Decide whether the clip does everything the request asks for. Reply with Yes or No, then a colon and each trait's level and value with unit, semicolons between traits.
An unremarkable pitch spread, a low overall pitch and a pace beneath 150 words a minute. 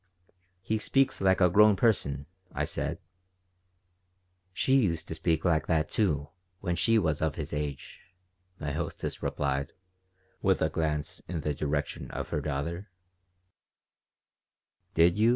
Yes: average, 4.4 semitones; very low, 80 Hz; slow, 135 wpm